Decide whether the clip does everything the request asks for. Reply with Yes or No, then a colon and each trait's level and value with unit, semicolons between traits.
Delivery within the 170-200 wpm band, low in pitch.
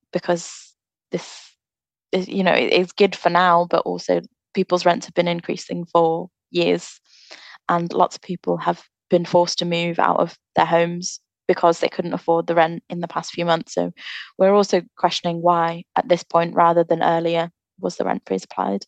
No: average, 185 wpm; medium, 170 Hz